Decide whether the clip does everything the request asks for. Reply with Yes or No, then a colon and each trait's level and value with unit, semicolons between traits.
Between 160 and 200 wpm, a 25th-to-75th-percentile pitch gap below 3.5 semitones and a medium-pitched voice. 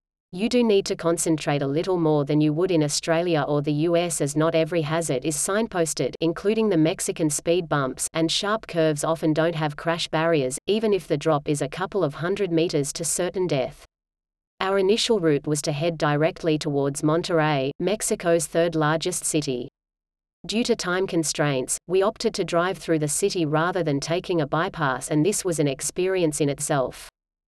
Yes: average, 185 wpm; average, 3.1 semitones; medium, 160 Hz